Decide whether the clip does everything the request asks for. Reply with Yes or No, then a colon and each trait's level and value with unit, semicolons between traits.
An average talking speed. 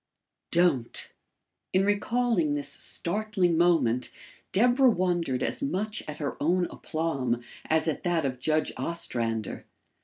No: slow, 120 wpm